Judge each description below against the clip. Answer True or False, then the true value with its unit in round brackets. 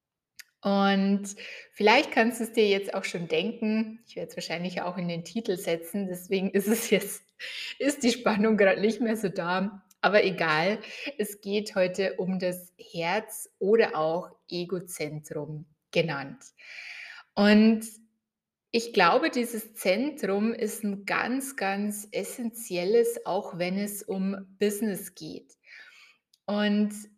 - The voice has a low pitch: False (200 Hz)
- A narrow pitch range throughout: False (3.1 semitones)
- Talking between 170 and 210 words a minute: False (130 wpm)